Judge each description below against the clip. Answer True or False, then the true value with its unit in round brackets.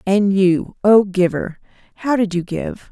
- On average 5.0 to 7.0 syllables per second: False (3.8 syllables/s)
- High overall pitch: True (195 Hz)